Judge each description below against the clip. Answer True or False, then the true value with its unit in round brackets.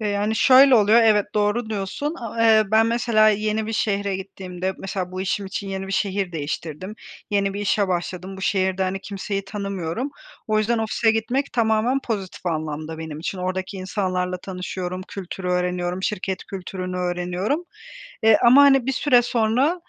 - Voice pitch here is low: False (200 Hz)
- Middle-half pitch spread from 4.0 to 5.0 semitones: False (3.2 semitones)